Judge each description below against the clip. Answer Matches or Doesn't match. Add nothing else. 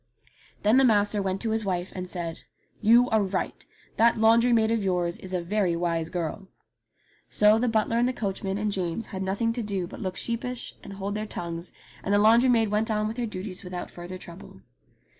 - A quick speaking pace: Matches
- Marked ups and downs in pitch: Doesn't match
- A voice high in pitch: Matches